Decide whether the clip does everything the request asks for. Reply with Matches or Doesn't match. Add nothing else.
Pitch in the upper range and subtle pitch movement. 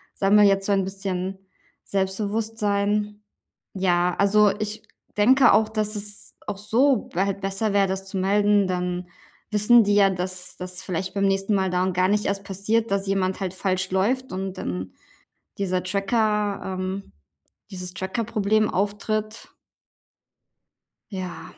Matches